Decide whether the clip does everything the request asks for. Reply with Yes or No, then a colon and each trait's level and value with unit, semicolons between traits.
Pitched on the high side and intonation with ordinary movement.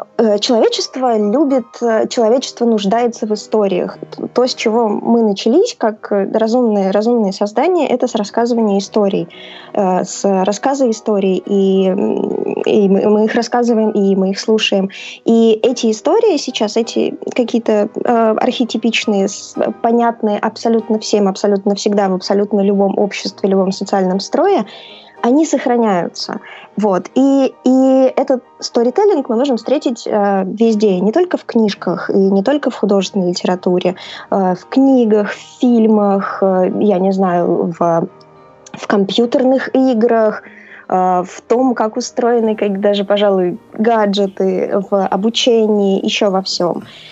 Yes: high, 220 Hz; average, 3.3 semitones